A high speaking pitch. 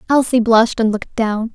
Yes: high, 230 Hz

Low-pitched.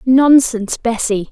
No: high, 240 Hz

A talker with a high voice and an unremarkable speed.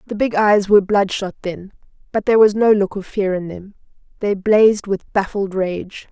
Yes: high, 200 Hz; average, 195 wpm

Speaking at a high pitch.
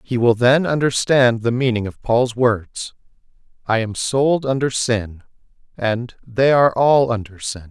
No: low, 120 Hz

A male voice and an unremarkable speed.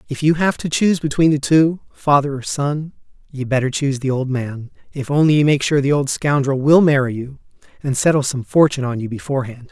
No: male; fast, 215 wpm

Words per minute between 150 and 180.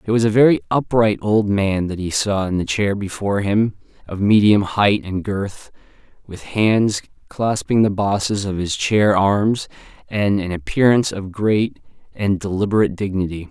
Yes: average, 165 wpm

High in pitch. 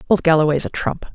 No: medium, 165 Hz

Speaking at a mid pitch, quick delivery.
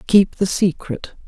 No: medium, 180 Hz; average, 140 wpm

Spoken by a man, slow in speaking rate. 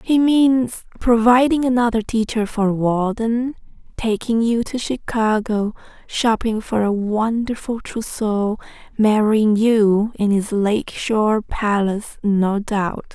No: female; slow, 115 wpm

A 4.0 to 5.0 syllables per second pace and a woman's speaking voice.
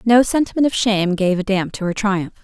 No: 5.8 syllables/s; female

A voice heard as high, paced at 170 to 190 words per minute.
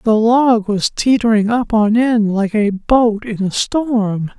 Yes: high, 220 Hz; average, 180 wpm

